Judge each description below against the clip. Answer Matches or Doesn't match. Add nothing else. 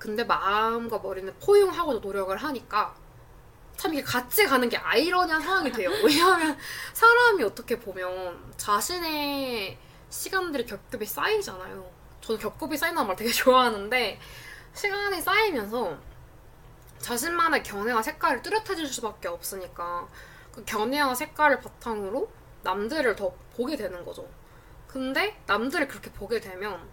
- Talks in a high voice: Matches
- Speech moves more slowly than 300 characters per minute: Doesn't match